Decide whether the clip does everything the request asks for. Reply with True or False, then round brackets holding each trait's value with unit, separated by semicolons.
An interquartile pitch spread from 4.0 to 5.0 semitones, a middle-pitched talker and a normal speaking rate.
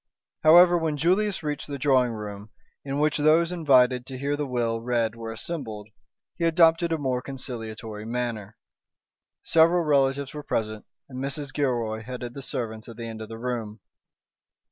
False (4.7 semitones; 130 Hz; 165 wpm)